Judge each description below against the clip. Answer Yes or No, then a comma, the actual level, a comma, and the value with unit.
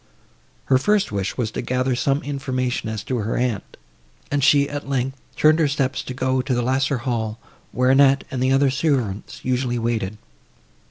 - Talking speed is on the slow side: No, average, 180 wpm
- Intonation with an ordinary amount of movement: No, narrow, 2.2 semitones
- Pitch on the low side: Yes, low, 130 Hz